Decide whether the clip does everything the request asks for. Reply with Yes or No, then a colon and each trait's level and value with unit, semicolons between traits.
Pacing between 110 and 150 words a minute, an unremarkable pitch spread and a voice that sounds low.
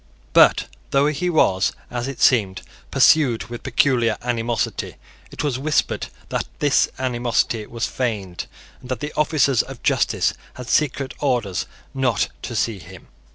Yes: average, 145 wpm; average, 3.4 semitones; low, 125 Hz